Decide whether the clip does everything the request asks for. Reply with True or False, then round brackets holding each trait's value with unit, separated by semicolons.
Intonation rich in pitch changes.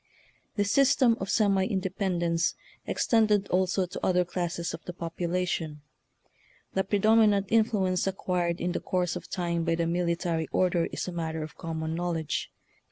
False (2.4 semitones)